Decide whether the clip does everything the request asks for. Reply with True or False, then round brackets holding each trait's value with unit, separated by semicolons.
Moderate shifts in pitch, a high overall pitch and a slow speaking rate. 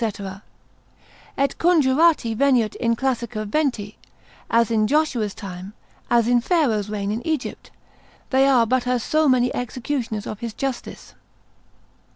True (4.1 semitones; 240 Hz; 130 wpm)